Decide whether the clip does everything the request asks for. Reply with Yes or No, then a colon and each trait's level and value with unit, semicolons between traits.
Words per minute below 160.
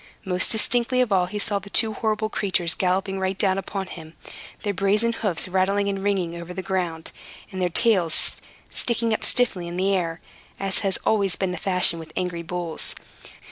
No: average, 185 wpm